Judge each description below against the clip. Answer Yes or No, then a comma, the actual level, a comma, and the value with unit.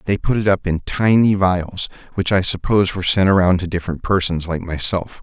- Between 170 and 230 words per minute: Yes, fast, 205 wpm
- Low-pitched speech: Yes, very low, 95 Hz